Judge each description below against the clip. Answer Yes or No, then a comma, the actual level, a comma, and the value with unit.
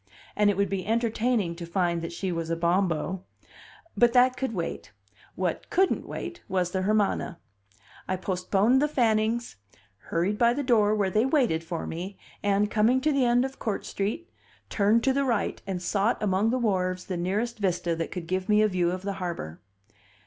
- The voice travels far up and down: No, average, 4.4 semitones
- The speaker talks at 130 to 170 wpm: No, average, 190 wpm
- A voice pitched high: Yes, high, 200 Hz